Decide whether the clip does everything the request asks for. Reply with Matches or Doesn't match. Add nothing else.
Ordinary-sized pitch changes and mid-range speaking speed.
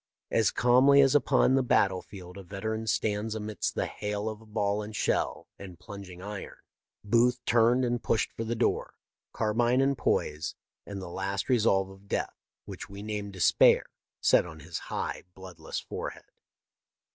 Matches